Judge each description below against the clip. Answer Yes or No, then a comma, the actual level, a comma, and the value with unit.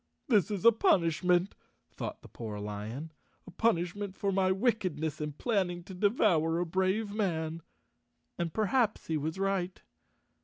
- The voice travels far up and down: No, average, 4.0 semitones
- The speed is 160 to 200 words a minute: No, average, 145 wpm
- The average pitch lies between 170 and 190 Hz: Yes, medium, 185 Hz